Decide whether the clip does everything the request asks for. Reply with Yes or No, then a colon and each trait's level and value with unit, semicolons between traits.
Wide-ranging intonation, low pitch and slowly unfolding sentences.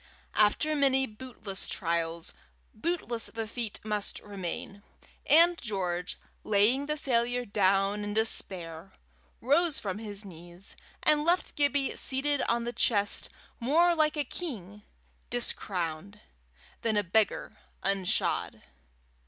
No: wide, 5.7 semitones; high, 215 Hz; slow, 115 wpm